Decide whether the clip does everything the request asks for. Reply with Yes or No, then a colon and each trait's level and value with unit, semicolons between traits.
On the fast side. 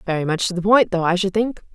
Yes: fast, 310 wpm